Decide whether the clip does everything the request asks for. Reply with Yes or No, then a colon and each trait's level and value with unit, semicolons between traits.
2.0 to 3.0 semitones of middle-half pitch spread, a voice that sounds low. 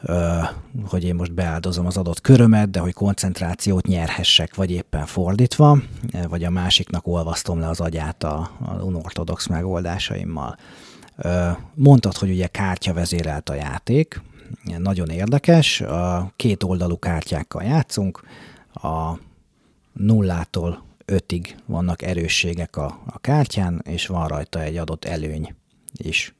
Yes: narrow, 2.6 semitones; very low, 90 Hz